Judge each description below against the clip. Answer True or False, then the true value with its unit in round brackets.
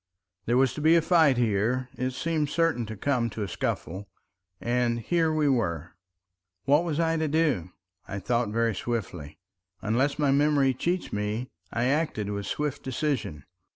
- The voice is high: False (125 Hz)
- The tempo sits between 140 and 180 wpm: True (165 wpm)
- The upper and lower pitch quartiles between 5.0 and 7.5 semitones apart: True (5.6 semitones)